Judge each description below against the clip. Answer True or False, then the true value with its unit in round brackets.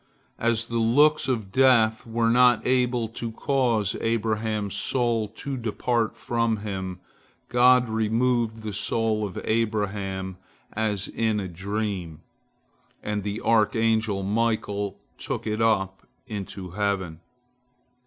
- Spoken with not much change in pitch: True (2.3 semitones)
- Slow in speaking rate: True (115 wpm)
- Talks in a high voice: False (110 Hz)